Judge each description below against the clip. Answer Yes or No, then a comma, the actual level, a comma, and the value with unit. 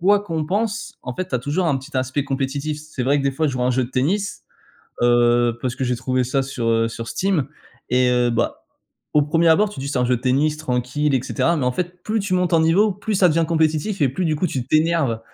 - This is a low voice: No, medium, 145 Hz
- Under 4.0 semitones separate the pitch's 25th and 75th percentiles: No, average, 5.1 semitones